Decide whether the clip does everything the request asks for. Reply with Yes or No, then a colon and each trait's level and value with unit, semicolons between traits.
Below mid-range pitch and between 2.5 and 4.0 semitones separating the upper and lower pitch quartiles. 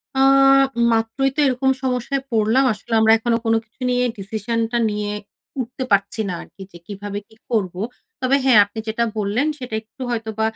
No: high, 225 Hz; average, 3.1 semitones